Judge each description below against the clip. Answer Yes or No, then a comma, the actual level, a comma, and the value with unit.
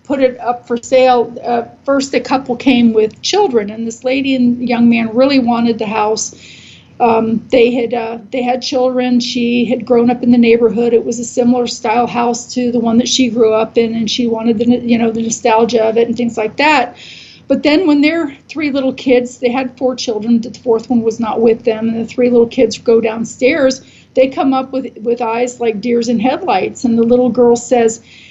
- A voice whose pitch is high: Yes, high, 240 Hz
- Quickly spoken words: Yes, fast, 220 wpm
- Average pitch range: No, narrow, 1.7 semitones